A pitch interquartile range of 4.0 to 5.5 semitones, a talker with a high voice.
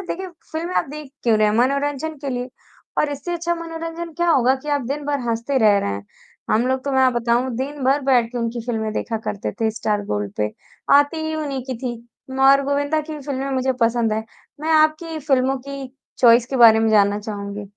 Yes: average, 4.3 semitones; very high, 265 Hz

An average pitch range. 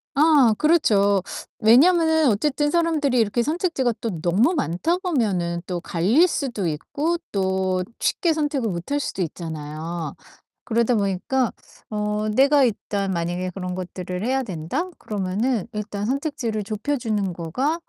No: wide, 7.7 semitones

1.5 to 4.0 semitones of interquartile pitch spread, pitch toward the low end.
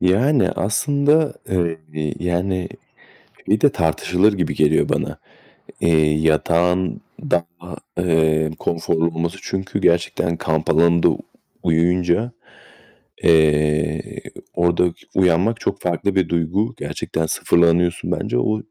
Yes: narrow, 2.5 semitones; very low, 85 Hz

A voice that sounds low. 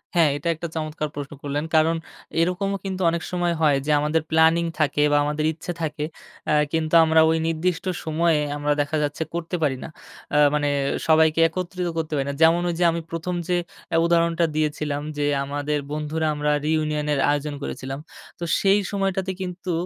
No: medium, 160 Hz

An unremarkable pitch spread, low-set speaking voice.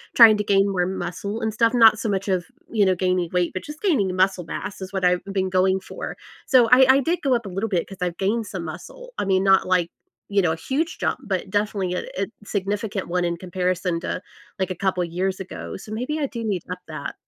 No: average, 3.3 semitones; high, 195 Hz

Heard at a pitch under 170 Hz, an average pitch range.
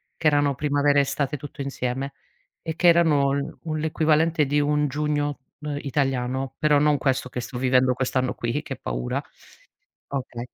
No: medium, 140 Hz; narrow, 2.2 semitones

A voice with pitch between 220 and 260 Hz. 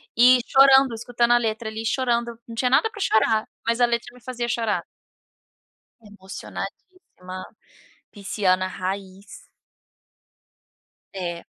Yes: high, 230 Hz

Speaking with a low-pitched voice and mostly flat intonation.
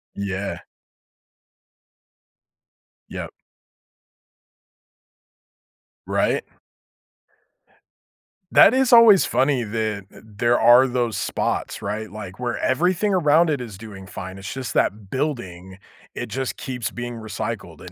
No: low, 120 Hz; average, 5.0 semitones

